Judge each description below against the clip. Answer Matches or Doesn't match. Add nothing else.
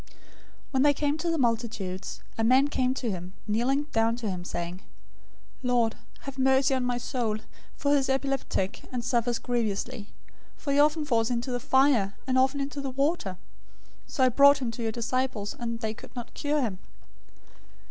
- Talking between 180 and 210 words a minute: Matches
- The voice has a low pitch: Doesn't match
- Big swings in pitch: Doesn't match